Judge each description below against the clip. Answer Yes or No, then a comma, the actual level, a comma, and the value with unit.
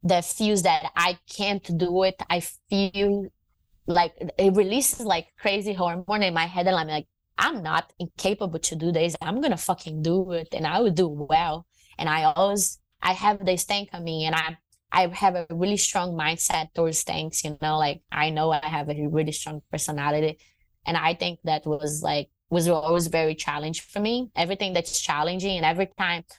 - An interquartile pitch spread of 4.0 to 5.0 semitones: No, average, 3.4 semitones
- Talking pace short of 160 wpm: No, average, 195 wpm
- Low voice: No, medium, 170 Hz